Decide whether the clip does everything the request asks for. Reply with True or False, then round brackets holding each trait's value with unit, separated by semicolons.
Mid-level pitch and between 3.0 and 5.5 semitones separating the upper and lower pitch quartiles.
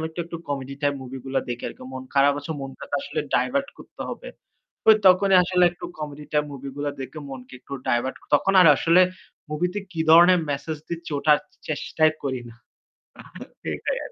True (150 Hz; 4.0 semitones)